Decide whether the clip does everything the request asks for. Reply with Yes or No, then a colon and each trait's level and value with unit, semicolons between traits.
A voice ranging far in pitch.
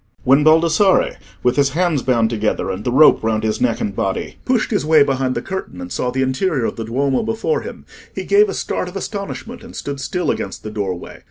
Yes: wide, 8.2 semitones